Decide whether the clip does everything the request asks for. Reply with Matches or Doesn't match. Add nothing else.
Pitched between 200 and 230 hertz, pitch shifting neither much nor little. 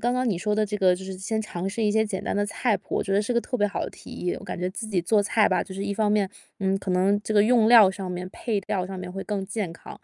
Doesn't match